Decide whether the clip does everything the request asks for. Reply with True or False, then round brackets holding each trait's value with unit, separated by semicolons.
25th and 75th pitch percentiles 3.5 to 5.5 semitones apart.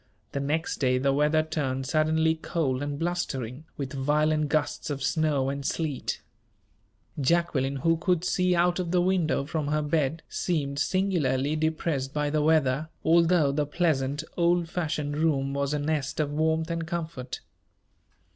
False (2.8 semitones)